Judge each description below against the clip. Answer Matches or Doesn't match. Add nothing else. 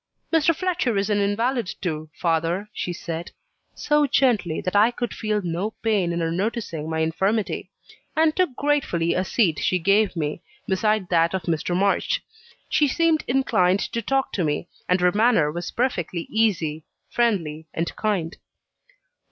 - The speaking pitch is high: Matches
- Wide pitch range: Matches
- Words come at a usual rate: Matches